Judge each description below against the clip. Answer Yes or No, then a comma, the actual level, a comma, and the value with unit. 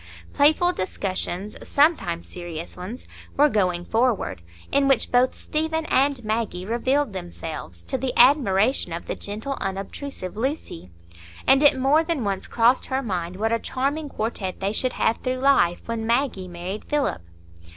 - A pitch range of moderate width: No, wide, 6.7 semitones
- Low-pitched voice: No, high, 230 Hz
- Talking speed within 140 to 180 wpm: Yes, average, 145 wpm